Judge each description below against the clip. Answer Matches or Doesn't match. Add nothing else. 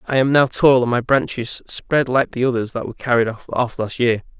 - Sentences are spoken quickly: Matches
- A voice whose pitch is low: Matches